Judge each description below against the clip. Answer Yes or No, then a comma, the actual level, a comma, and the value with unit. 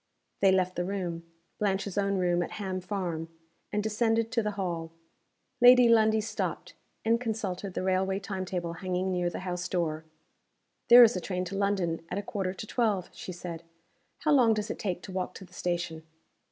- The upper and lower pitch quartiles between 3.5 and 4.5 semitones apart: No, average, 2.9 semitones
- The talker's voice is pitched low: No, high, 190 Hz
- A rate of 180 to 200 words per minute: Yes, average, 190 wpm